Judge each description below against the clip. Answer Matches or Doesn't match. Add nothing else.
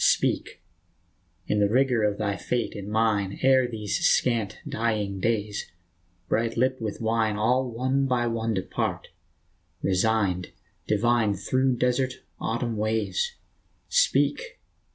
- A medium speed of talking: Doesn't match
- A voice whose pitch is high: Doesn't match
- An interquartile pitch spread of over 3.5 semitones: Doesn't match